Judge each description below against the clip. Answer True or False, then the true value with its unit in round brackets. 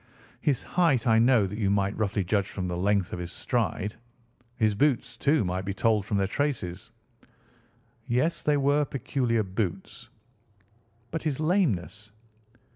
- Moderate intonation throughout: False (5.8 semitones)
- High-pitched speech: False (110 Hz)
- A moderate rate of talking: True (150 wpm)